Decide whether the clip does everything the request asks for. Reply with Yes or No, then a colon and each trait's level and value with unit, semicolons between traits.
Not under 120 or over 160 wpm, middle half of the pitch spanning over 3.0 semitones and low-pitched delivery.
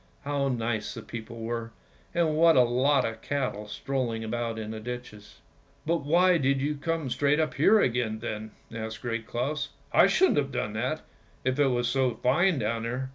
No: average, 200 wpm; average, 4.1 semitones; low, 125 Hz